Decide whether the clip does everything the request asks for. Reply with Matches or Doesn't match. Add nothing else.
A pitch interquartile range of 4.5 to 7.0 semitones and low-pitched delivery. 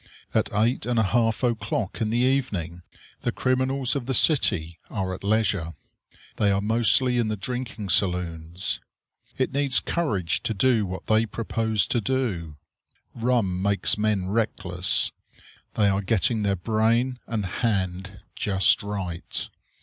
Doesn't match